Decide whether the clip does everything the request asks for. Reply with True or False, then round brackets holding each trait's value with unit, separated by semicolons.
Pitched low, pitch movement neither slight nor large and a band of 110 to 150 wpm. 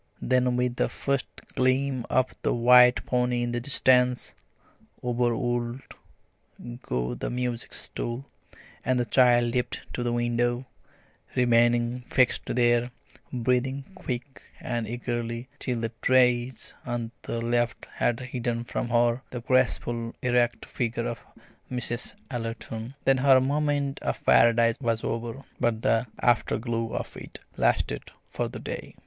False (120 Hz; 1.2 semitones; 135 wpm)